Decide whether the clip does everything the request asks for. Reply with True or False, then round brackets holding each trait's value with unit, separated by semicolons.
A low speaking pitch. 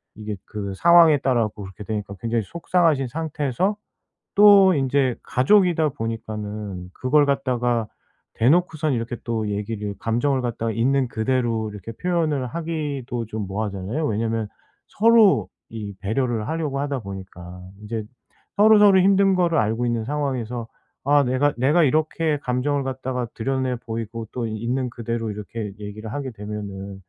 True (120 Hz)